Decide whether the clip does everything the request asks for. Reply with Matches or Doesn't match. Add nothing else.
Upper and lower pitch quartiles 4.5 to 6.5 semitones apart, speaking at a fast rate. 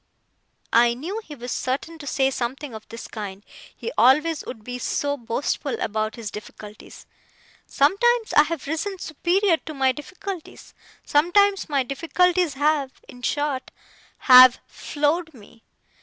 Doesn't match